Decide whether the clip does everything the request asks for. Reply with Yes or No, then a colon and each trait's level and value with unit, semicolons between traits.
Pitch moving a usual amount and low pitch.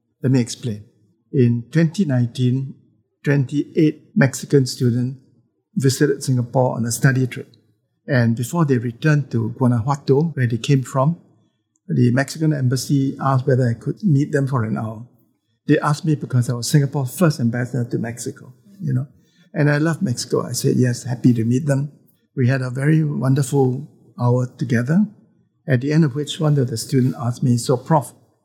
Yes: average, 3.2 semitones; low, 130 Hz